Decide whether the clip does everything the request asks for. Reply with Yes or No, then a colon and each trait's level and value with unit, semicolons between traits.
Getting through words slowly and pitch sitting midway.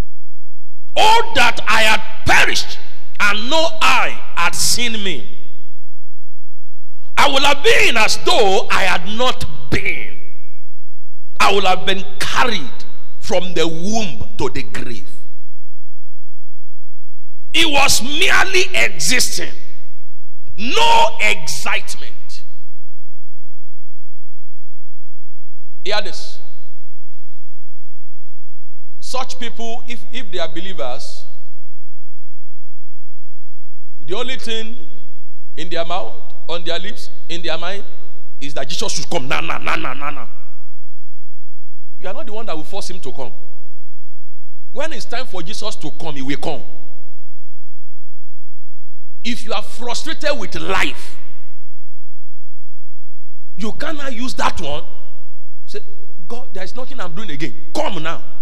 Yes: slow, 115 wpm; medium, 175 Hz